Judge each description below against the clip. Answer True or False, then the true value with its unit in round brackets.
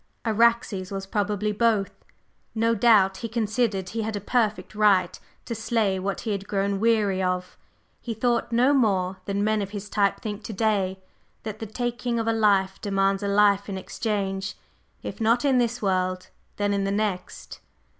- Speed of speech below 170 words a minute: False (175 wpm)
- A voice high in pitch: True (205 Hz)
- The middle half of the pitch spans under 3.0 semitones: True (2.5 semitones)